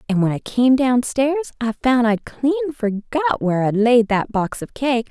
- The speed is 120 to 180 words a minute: No, average, 200 wpm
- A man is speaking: No, female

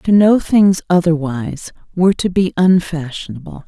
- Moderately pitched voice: Yes, medium, 175 Hz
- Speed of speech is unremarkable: No, slow, 130 wpm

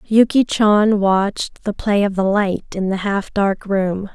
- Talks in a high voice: Yes, high, 200 Hz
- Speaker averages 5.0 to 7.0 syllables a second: No, 3.8 syllables/s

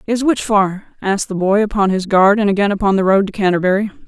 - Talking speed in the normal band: No, fast, 235 wpm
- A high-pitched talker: Yes, high, 200 Hz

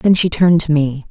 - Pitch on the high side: No, medium, 160 Hz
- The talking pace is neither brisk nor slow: No, fast, 270 wpm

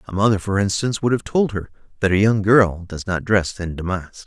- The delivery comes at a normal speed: No, fast, 240 wpm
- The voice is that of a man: Yes, male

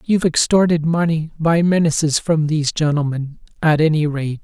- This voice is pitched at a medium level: Yes, medium, 155 Hz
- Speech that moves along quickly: No, average, 150 wpm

